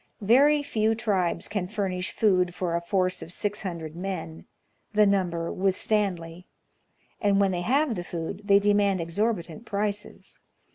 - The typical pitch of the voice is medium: No, high, 195 Hz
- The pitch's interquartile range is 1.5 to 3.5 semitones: Yes, average, 3.0 semitones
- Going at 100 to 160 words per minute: Yes, average, 150 wpm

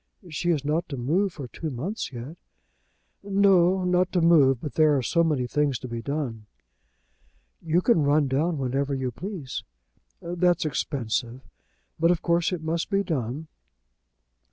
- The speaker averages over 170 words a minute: No, average, 155 wpm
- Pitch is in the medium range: Yes, medium, 155 Hz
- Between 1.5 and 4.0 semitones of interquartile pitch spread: No, average, 4.6 semitones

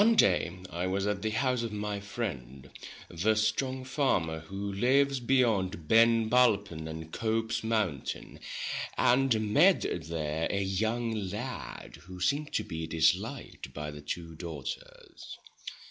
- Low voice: Yes, low, 100 Hz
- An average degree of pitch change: No, wide, 5.9 semitones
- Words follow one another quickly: No, average, 140 wpm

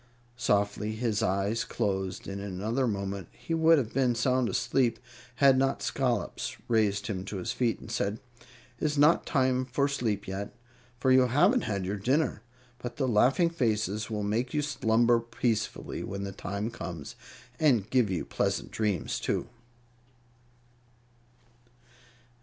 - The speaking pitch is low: Yes, low, 115 Hz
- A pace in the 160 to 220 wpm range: No, average, 150 wpm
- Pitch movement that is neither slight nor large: Yes, average, 4.2 semitones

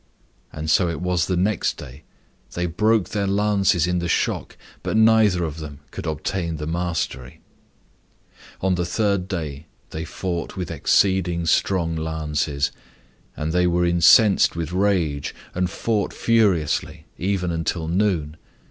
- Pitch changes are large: No, average, 3.2 semitones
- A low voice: Yes, very low, 85 Hz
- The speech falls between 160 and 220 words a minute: No, average, 140 wpm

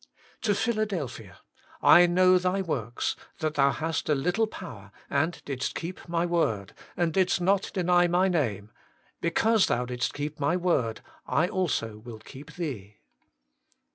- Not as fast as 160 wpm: Yes, average, 150 wpm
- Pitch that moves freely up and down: Yes, wide, 6.1 semitones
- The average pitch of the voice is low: No, medium, 165 Hz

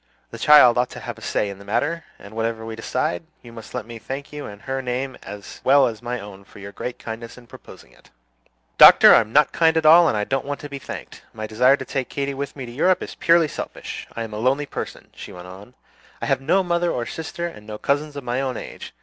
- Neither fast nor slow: No, fast, 255 wpm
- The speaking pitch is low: Yes, low, 125 Hz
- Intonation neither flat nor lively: Yes, average, 4.3 semitones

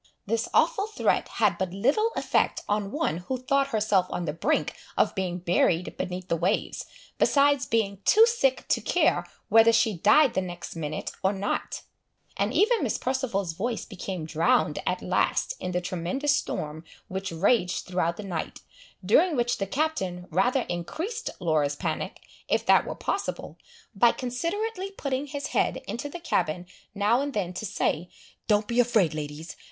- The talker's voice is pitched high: Yes, high, 205 Hz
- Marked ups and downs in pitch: Yes, wide, 7.4 semitones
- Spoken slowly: No, average, 165 wpm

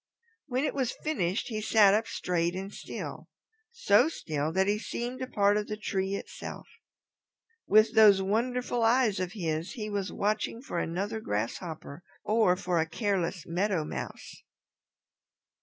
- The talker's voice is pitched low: No, high, 205 Hz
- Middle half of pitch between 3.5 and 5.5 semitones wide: Yes, average, 3.8 semitones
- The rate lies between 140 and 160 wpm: Yes, average, 150 wpm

